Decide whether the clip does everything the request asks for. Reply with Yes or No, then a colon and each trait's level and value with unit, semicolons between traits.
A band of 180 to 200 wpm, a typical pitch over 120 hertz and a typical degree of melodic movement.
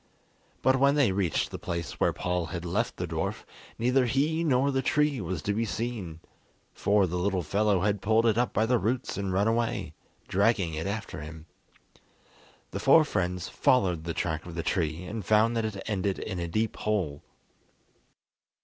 No: average, 185 wpm; low, 100 Hz; average, 4.7 semitones